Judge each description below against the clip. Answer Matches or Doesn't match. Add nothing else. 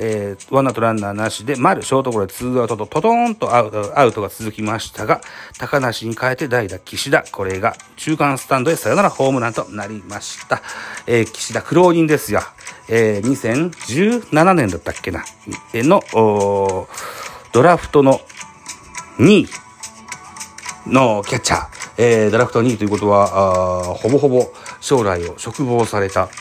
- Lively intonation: Doesn't match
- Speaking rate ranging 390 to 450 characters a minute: Doesn't match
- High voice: Doesn't match